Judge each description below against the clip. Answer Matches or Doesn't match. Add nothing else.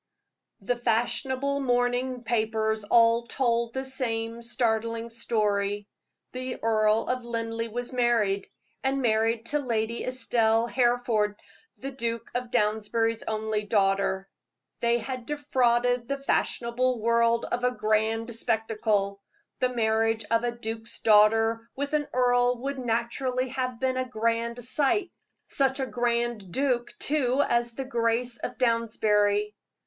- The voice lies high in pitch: Matches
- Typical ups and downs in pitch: Doesn't match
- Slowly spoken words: Matches